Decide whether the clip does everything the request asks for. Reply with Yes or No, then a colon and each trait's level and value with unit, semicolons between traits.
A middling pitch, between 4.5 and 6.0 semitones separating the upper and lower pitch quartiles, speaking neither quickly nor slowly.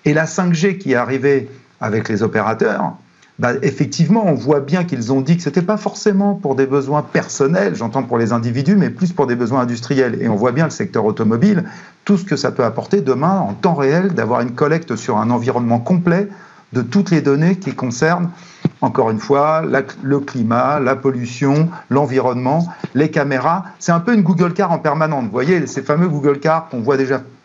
Yes: medium, 145 Hz; average, 5.3 semitones; average, 205 wpm